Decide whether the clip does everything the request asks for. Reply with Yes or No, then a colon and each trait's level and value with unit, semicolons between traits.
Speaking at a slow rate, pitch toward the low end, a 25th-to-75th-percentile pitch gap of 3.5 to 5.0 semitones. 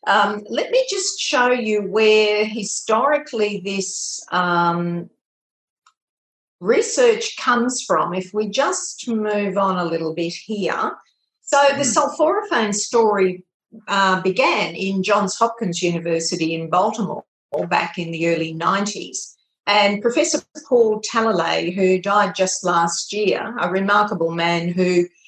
No: slow, 125 wpm; high, 205 Hz; average, 4.4 semitones